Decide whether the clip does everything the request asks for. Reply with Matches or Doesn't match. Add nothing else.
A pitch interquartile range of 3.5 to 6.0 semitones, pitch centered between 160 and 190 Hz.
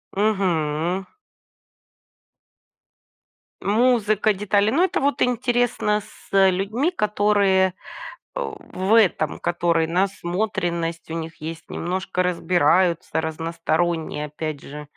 Matches